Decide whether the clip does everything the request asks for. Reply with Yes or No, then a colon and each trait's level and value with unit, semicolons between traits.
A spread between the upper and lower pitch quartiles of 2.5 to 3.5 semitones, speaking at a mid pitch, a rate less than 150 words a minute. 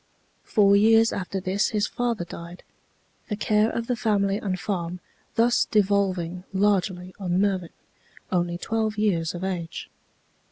No: average, 2.9 semitones; high, 195 Hz; slow, 135 wpm